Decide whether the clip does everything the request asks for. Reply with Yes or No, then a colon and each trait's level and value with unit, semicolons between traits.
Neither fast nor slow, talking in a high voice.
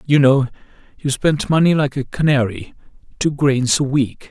No: average, 165 wpm; low, 135 Hz